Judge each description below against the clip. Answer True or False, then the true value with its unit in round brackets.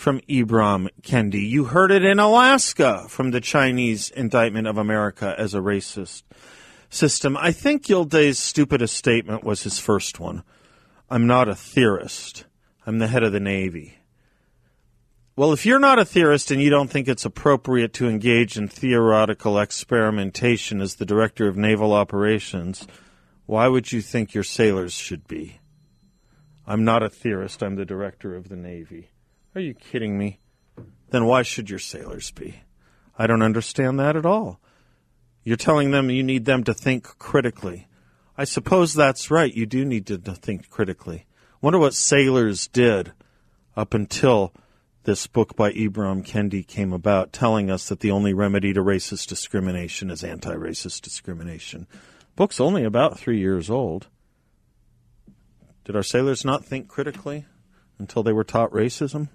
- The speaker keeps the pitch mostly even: False (4.8 semitones)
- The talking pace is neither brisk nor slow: True (155 wpm)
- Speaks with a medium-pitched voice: False (115 Hz)